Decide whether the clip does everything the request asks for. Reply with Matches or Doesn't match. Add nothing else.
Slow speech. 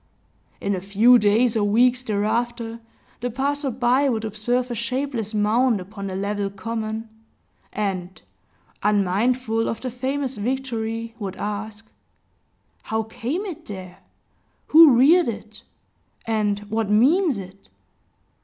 Matches